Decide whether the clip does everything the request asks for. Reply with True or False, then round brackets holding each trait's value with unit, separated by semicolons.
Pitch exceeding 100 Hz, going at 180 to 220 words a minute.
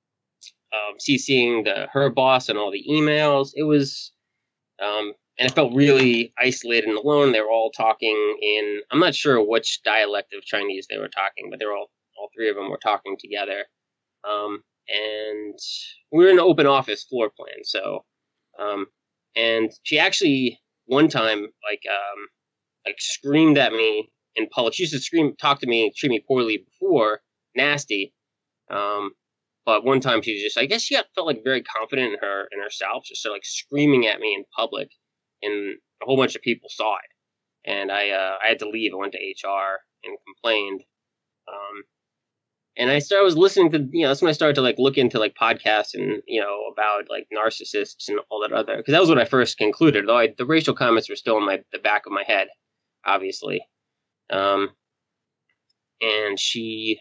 True (135 Hz; 190 wpm)